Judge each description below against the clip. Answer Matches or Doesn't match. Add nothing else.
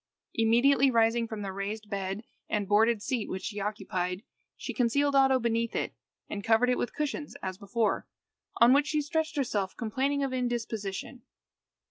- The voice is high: Matches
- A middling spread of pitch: Matches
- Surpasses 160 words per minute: Doesn't match